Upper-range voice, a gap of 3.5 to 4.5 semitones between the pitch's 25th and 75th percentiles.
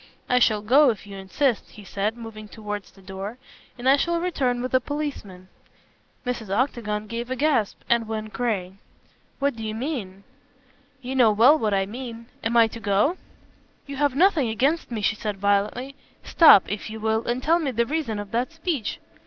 Yes: high, 230 Hz; average, 4.2 semitones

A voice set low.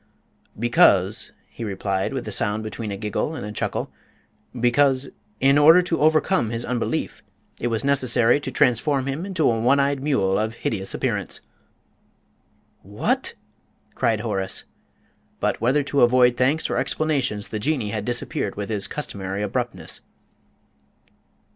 Yes: low, 120 Hz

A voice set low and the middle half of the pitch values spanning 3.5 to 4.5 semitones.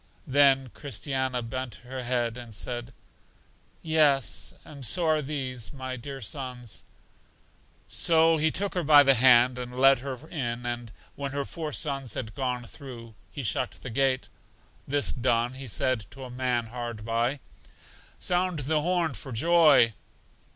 No: low, 130 Hz; average, 3.0 semitones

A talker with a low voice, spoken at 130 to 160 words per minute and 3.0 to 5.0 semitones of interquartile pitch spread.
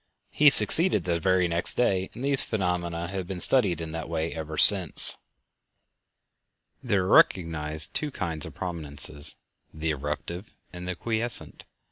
Yes: very low, 90 Hz; average, 140 wpm; average, 3.4 semitones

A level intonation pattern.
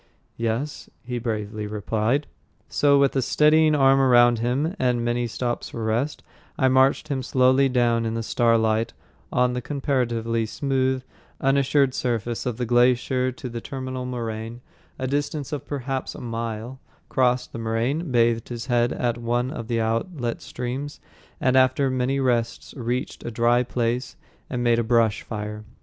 Yes: narrow, 2.3 semitones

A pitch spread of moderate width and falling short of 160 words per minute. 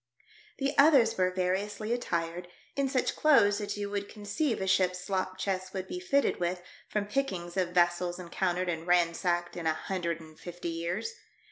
No: average, 3.1 semitones; average, 170 wpm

